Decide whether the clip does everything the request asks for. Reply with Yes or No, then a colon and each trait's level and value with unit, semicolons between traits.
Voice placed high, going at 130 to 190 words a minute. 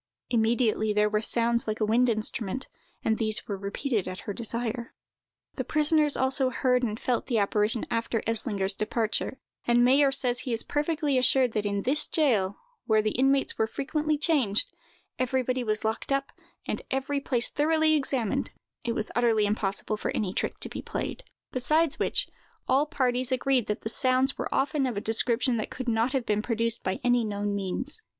Yes: high, 240 Hz; average, 180 wpm